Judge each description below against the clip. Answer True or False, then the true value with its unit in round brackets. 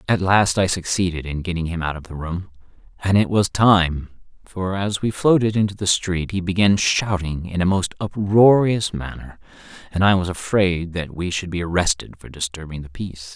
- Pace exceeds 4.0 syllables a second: True (5.0 syllables/s)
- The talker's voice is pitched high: False (90 Hz)